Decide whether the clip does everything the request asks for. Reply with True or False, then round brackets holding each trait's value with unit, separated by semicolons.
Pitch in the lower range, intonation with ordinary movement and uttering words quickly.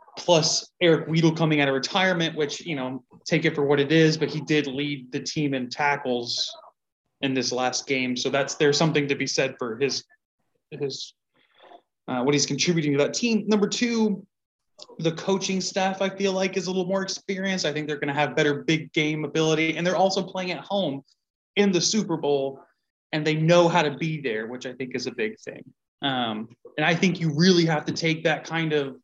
False (155 Hz; 4.7 semitones; 215 wpm)